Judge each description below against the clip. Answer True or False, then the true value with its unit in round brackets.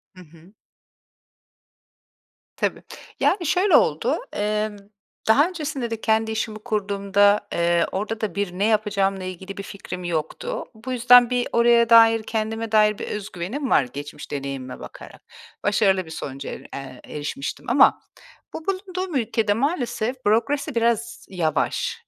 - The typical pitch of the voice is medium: False (215 Hz)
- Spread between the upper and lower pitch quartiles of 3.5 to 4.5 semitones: True (4.2 semitones)